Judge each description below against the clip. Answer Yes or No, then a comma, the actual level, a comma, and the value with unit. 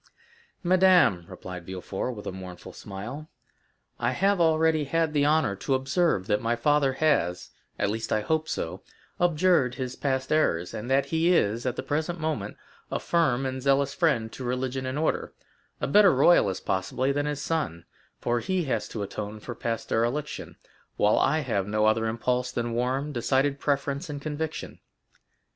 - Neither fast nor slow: Yes, average, 160 wpm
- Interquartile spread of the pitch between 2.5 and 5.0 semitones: No, wide, 5.5 semitones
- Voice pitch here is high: No, low, 130 Hz